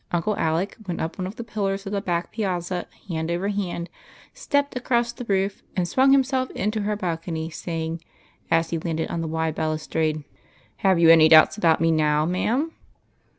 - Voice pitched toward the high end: No, medium, 175 Hz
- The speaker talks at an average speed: Yes, average, 190 wpm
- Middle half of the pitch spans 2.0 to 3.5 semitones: No, average, 4.3 semitones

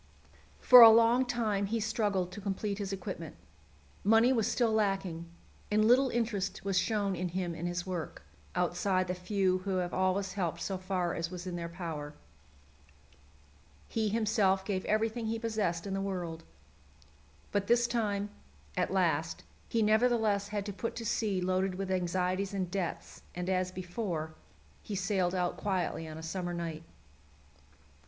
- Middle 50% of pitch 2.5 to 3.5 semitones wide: Yes, average, 3.1 semitones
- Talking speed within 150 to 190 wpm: Yes, average, 160 wpm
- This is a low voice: No, high, 195 Hz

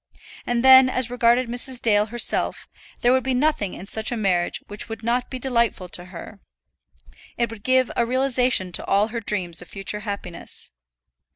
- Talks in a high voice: Yes, high, 235 Hz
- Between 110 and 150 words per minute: No, average, 180 wpm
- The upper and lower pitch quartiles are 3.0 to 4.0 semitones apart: Yes, average, 3.7 semitones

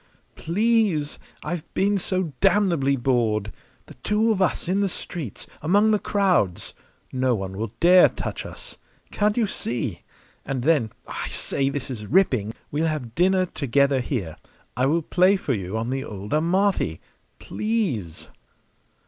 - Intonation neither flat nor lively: No, wide, 8.1 semitones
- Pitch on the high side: No, medium, 150 Hz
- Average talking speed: Yes, average, 150 wpm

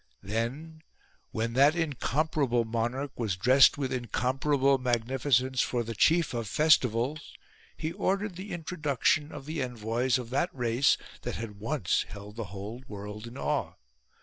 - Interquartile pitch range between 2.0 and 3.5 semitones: No, average, 4.4 semitones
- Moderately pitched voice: No, low, 125 Hz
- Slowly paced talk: No, average, 145 wpm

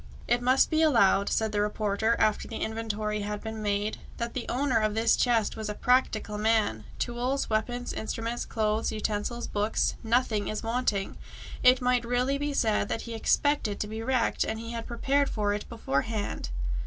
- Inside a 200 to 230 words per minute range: No, average, 175 wpm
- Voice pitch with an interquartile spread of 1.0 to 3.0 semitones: Yes, narrow, 2.5 semitones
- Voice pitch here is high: Yes, high, 225 Hz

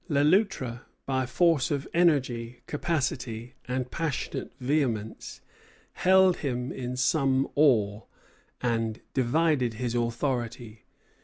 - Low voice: Yes, low, 130 Hz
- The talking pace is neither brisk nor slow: No, slow, 100 wpm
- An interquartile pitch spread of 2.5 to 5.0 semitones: Yes, average, 3.9 semitones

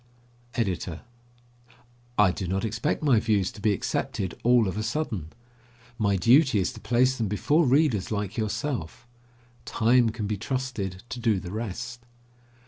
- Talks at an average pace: Yes, average, 150 wpm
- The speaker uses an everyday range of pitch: Yes, average, 3.8 semitones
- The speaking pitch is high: No, low, 110 Hz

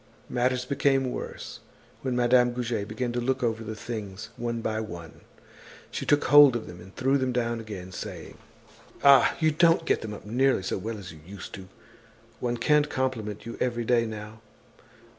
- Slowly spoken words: No, average, 185 wpm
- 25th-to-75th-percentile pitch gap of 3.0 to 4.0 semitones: Yes, average, 3.3 semitones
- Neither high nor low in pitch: No, low, 120 Hz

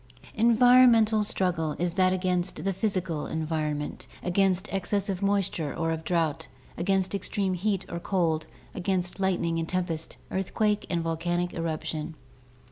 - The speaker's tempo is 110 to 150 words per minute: Yes, slow, 135 wpm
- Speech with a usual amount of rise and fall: Yes, average, 3.0 semitones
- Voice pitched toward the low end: No, medium, 180 Hz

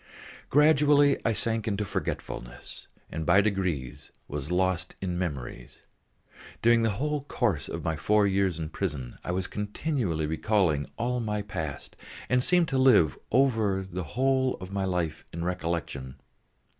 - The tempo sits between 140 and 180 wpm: Yes, average, 150 wpm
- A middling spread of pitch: No, wide, 6.2 semitones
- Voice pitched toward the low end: Yes, very low, 95 Hz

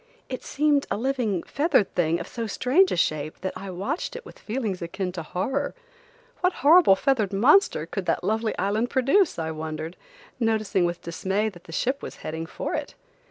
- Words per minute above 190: No, average, 185 wpm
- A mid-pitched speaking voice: No, high, 210 Hz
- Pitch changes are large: Yes, wide, 7.4 semitones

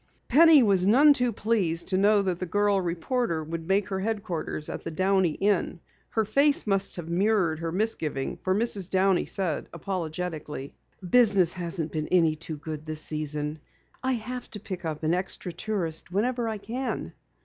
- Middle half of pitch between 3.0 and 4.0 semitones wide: No, average, 4.6 semitones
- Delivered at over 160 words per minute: Yes, average, 170 wpm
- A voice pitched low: No, medium, 185 Hz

